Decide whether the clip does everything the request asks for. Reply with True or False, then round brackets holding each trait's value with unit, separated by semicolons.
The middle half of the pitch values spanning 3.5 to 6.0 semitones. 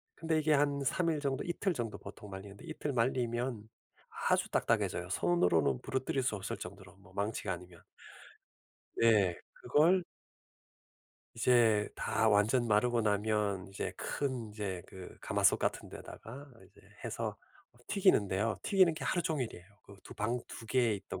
True (5.4 semitones)